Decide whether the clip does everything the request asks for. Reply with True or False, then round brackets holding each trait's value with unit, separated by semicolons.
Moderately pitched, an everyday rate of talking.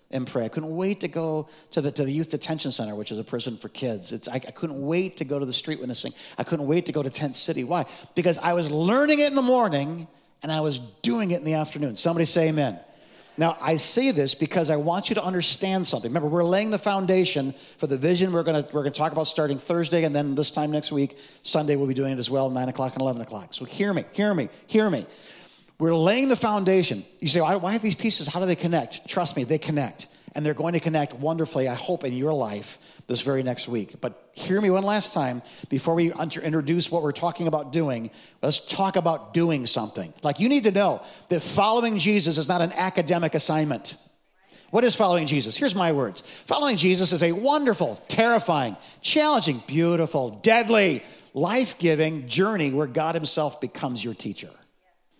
False (160 Hz; 220 wpm)